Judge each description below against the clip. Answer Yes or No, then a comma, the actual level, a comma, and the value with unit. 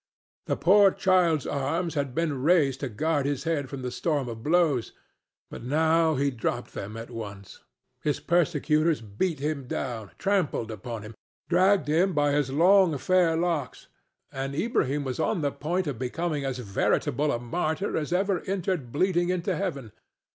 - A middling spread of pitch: Yes, average, 4.9 semitones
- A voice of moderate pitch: Yes, medium, 150 Hz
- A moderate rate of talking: Yes, average, 165 wpm